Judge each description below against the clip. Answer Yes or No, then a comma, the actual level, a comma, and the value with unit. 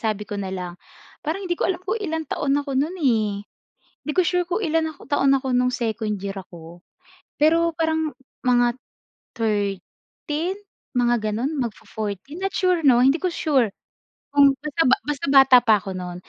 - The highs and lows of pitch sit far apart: Yes, wide, 6.9 semitones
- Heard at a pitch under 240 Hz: No, very high, 270 Hz